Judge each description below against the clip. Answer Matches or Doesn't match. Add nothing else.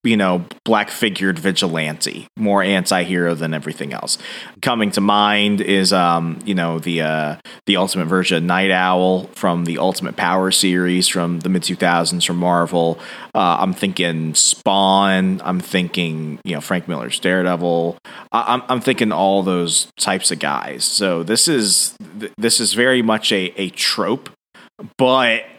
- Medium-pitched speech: Doesn't match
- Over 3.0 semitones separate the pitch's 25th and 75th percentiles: Doesn't match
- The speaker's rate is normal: Matches